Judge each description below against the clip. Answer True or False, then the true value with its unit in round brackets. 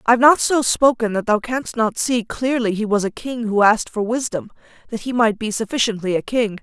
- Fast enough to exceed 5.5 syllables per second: False (5.4 syllables/s)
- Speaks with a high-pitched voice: True (225 Hz)